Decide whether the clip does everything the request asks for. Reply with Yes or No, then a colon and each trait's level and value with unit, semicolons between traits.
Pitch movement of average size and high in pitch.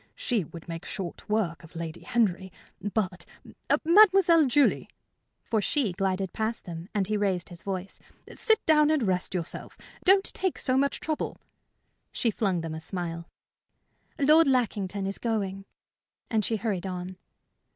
No: wide, 6.1 semitones; high, 200 Hz